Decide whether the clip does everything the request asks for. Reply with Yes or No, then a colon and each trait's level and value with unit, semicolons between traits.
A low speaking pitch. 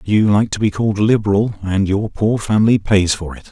Yes: low, 105 Hz